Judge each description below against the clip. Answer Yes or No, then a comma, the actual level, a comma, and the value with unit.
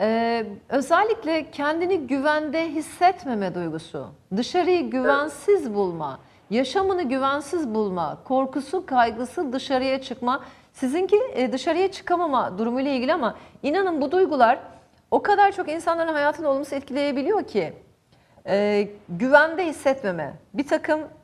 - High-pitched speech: Yes, very high, 285 Hz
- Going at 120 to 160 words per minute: No, average, 105 wpm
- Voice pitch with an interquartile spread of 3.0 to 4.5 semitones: No, average, 5.2 semitones